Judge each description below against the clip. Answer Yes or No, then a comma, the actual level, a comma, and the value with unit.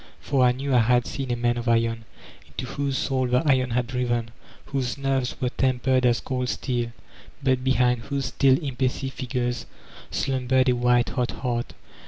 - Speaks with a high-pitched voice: No, low, 125 Hz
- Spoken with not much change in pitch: Yes, narrow, 1.5 semitones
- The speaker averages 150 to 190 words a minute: Yes, average, 175 wpm